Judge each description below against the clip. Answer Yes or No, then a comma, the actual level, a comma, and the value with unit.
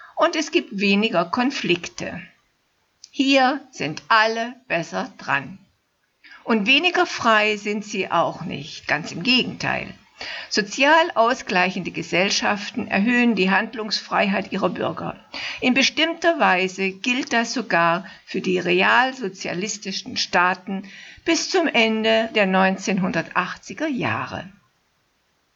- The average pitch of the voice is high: Yes, high, 220 Hz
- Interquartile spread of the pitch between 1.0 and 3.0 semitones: No, average, 5.1 semitones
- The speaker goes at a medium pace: No, slow, 105 wpm